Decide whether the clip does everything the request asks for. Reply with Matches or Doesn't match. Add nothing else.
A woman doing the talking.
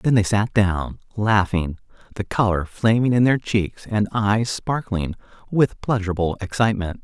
Doesn't match